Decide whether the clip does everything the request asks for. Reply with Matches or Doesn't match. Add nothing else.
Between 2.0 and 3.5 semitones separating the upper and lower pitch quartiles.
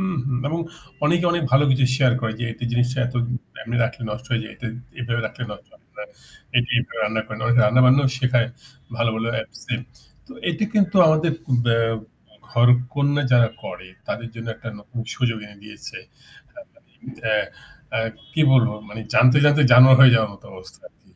Matches